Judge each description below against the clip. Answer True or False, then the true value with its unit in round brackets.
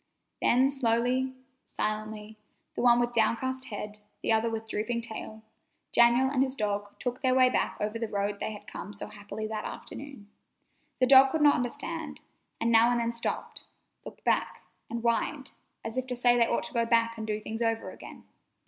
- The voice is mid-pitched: False (235 Hz)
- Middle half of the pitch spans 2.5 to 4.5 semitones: True (2.8 semitones)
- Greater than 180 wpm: True (190 wpm)